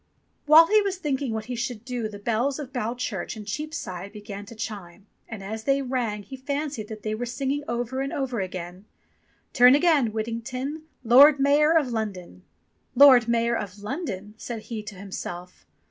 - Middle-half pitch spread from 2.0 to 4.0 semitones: No, average, 4.6 semitones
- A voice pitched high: Yes, high, 235 Hz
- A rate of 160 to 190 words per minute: Yes, average, 180 wpm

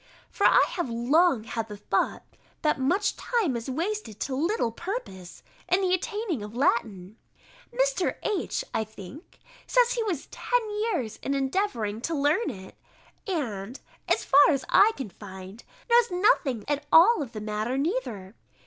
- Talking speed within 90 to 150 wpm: No, average, 160 wpm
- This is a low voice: No, very high, 280 Hz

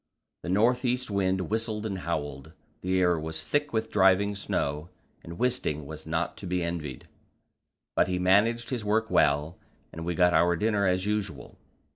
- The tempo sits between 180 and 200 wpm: No, average, 170 wpm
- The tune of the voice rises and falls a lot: No, average, 4.6 semitones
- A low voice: Yes, very low, 95 Hz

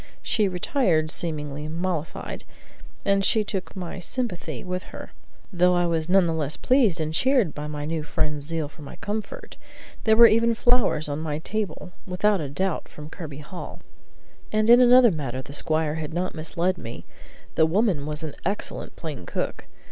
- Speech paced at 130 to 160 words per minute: No, average, 175 wpm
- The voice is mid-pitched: Yes, medium, 170 Hz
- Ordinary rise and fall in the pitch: Yes, average, 4.9 semitones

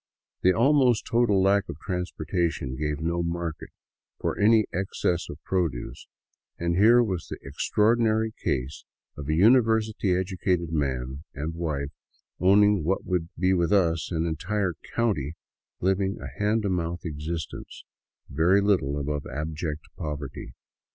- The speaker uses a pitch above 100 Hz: No, very low, 90 Hz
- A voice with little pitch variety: No, average, 4.6 semitones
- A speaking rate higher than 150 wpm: No, slow, 135 wpm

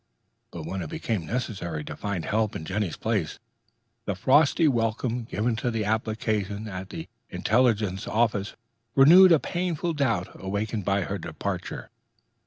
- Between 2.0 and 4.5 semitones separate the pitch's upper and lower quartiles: Yes, average, 3.8 semitones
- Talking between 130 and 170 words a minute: Yes, average, 140 wpm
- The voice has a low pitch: Yes, low, 110 Hz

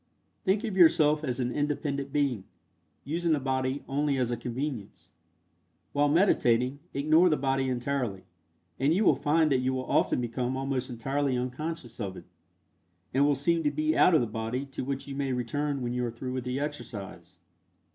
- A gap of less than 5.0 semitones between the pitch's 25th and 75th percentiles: Yes, average, 2.9 semitones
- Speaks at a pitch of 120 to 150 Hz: Yes, low, 135 Hz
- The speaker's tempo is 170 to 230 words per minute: Yes, average, 185 wpm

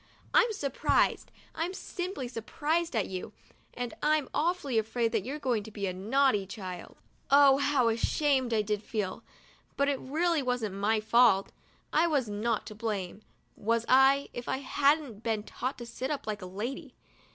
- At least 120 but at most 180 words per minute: Yes, average, 175 wpm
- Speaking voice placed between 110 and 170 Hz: No, high, 245 Hz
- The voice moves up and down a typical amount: Yes, average, 4.8 semitones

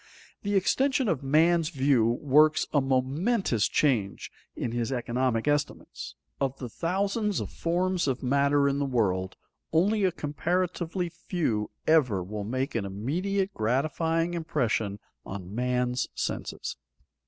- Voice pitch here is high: No, medium, 140 Hz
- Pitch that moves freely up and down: Yes, wide, 6.1 semitones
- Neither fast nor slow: No, slow, 130 wpm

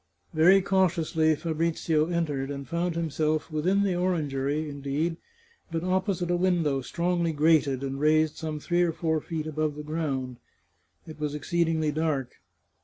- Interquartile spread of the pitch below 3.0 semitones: Yes, narrow, 2.5 semitones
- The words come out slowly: No, average, 150 wpm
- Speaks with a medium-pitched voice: Yes, medium, 160 Hz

